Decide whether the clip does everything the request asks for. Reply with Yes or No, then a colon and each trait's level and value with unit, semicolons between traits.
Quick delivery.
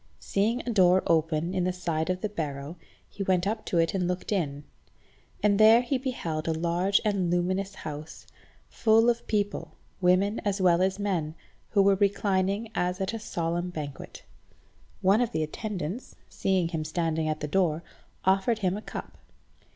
No: average, 175 wpm